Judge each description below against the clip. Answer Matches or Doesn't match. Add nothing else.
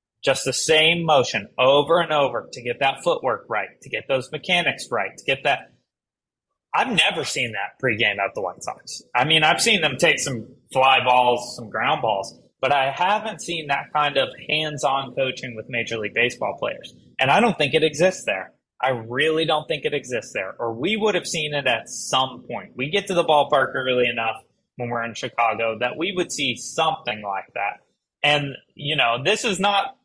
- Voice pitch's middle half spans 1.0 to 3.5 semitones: Doesn't match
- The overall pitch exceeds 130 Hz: Matches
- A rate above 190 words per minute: Matches